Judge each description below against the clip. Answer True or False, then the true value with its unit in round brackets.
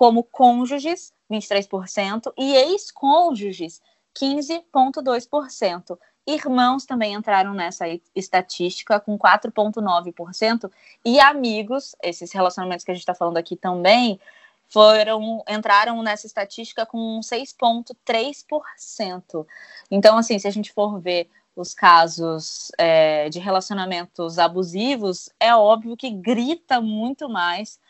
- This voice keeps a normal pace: False (110 wpm)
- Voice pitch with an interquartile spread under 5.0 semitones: False (5.3 semitones)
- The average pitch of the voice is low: False (215 Hz)